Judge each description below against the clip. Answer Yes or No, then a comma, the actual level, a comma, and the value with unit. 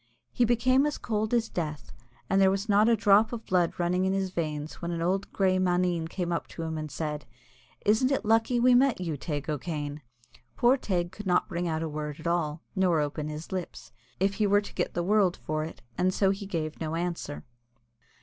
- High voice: No, medium, 180 Hz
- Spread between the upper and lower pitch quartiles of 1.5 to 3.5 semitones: No, average, 4.3 semitones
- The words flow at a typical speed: No, fast, 225 wpm